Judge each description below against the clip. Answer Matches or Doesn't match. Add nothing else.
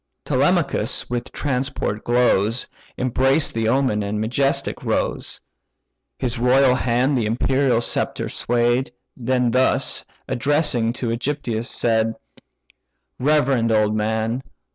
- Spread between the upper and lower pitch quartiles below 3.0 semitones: Matches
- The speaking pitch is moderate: Doesn't match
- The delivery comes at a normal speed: Doesn't match